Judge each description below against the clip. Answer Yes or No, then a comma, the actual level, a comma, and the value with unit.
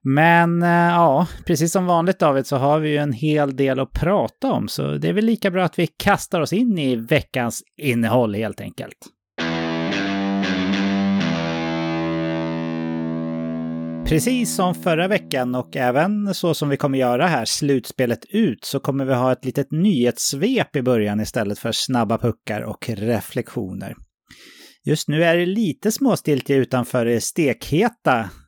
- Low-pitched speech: Yes, low, 130 Hz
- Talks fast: No, average, 150 wpm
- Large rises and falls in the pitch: Yes, wide, 8.3 semitones